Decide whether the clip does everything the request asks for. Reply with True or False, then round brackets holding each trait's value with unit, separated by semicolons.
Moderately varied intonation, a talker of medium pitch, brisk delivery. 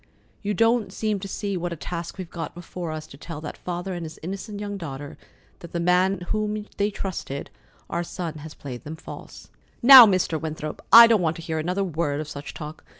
True (4.0 semitones; 175 Hz; 215 wpm)